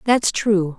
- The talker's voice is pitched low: No, high, 200 Hz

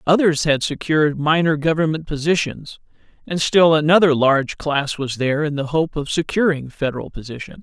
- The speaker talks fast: No, average, 155 wpm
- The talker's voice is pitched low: No, medium, 150 Hz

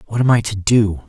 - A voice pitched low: Yes, low, 110 Hz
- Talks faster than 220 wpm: Yes, fast, 280 wpm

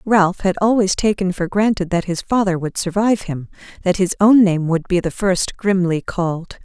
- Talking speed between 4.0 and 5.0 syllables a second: Yes, 4.9 syllables/s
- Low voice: No, high, 190 Hz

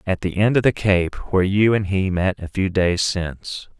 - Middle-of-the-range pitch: No, very low, 95 Hz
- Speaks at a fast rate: Yes, fast, 235 wpm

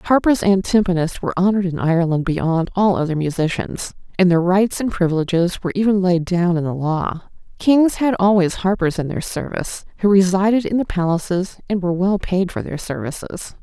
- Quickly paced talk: No, average, 185 wpm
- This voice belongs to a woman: Yes, female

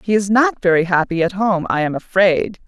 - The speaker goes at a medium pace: No, fast, 225 wpm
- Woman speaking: Yes, female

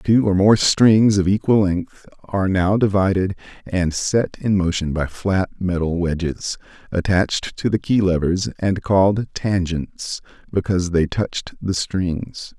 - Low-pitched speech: Yes, very low, 95 Hz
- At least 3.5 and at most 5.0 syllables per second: Yes, 4.1 syllables/s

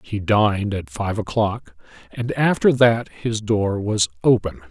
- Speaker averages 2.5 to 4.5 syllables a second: Yes, 4.0 syllables/s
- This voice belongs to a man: Yes, male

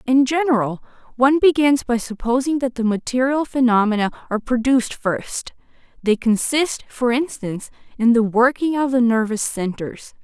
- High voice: Yes, high, 245 Hz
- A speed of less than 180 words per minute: Yes, average, 140 wpm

